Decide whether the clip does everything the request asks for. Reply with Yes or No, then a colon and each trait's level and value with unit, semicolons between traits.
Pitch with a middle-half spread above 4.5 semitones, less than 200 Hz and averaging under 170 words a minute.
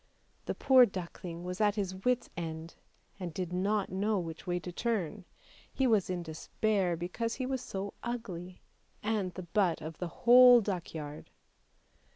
No: average, 3.9 semitones; medium, 185 Hz; average, 160 wpm